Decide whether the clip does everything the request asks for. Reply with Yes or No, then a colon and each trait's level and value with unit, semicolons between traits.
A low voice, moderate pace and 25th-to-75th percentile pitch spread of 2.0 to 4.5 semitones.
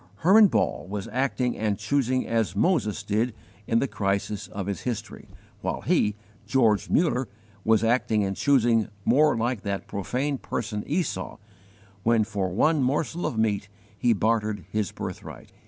Yes: low, 115 Hz; average, 150 wpm; average, 3.9 semitones